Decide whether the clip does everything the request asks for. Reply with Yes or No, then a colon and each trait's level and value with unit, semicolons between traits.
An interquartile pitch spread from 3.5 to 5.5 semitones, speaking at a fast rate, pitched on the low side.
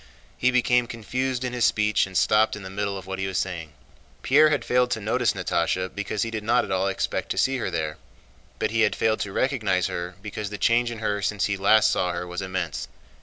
Yes: average, 4.1 semitones; fast, 235 wpm; low, 105 Hz